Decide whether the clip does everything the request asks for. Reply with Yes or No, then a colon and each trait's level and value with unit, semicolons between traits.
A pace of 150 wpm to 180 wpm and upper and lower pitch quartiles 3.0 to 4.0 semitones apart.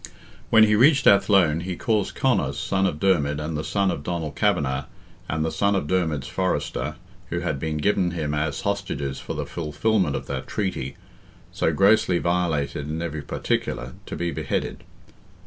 No: average, 170 wpm; average, 4.7 semitones